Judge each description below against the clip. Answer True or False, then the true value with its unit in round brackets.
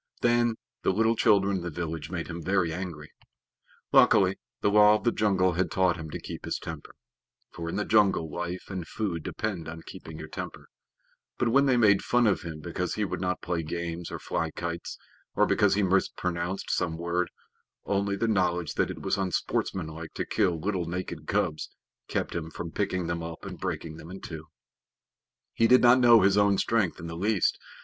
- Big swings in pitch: False (3.5 semitones)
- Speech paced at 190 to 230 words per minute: True (195 wpm)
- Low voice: True (90 Hz)